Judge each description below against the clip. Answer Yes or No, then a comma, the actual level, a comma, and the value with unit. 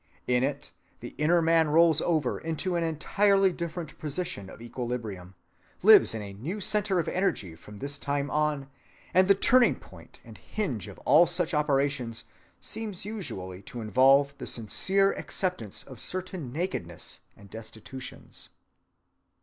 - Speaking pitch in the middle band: Yes, medium, 145 Hz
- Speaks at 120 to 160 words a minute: Yes, average, 140 wpm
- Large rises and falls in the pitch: Yes, wide, 7.0 semitones